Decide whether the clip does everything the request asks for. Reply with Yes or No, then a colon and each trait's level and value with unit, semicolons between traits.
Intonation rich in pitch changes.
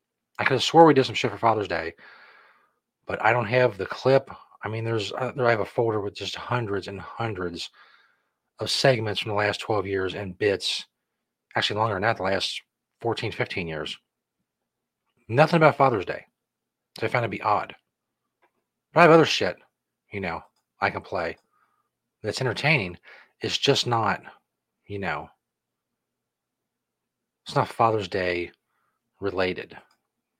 No: average, 4.1 semitones